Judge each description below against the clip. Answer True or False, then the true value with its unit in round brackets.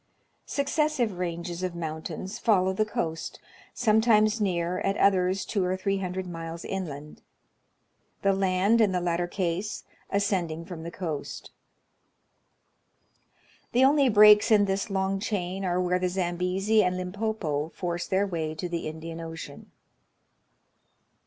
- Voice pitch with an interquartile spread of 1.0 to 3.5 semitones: True (3.0 semitones)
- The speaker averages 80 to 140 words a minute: True (135 wpm)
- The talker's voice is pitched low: False (185 Hz)